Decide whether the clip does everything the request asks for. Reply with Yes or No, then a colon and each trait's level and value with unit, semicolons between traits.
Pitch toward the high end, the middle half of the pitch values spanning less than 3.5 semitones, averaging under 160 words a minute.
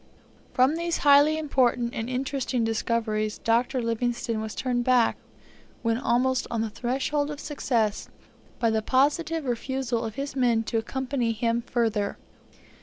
Yes: high, 245 Hz; average, 2.8 semitones; average, 140 wpm